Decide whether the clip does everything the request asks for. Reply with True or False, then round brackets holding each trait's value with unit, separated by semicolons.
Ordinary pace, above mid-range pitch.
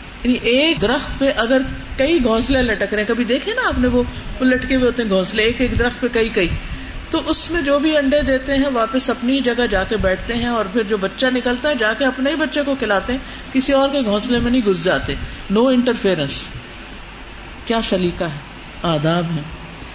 False (215 wpm; 245 Hz)